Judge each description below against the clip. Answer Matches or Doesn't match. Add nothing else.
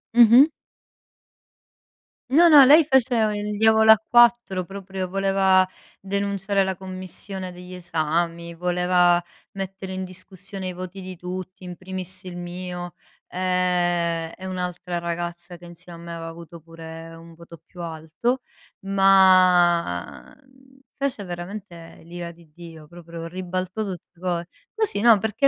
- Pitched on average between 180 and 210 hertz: Matches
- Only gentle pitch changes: Matches